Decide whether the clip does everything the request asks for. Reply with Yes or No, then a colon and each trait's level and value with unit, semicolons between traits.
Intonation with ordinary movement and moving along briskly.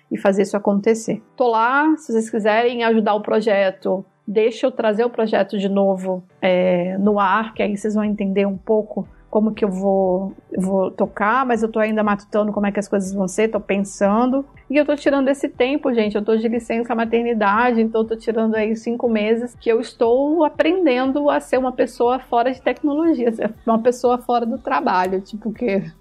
Yes: average, 3.4 semitones; fast, 200 wpm